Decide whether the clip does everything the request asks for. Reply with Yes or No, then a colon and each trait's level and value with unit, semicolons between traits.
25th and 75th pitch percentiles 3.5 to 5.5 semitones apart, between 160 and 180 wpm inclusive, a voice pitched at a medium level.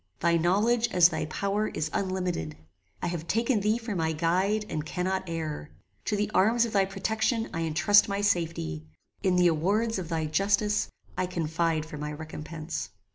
Yes: average, 4.4 semitones; average, 175 wpm; medium, 180 Hz